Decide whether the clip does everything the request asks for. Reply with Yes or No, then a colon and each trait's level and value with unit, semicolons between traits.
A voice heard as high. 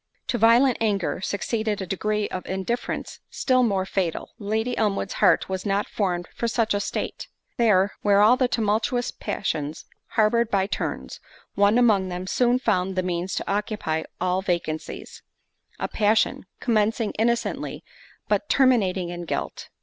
Yes: high, 205 Hz